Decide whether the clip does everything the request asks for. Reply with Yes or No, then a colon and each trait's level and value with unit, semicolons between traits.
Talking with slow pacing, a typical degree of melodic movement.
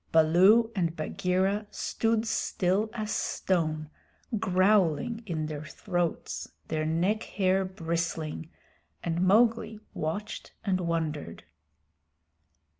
Yes: slow, 95 wpm; average, 4.4 semitones